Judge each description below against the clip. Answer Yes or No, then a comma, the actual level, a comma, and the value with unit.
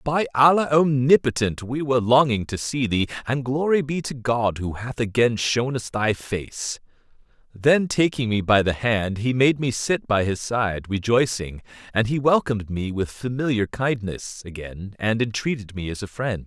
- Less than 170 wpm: No, average, 180 wpm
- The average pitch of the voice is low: Yes, low, 120 Hz